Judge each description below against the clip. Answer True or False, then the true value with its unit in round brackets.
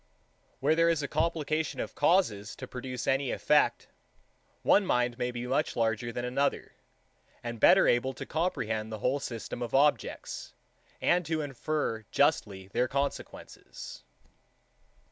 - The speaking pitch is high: False (130 Hz)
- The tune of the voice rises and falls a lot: False (4.4 semitones)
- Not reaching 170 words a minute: True (145 wpm)